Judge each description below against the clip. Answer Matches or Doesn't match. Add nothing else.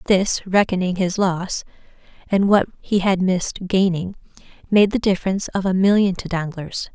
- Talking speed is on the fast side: Doesn't match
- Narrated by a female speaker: Matches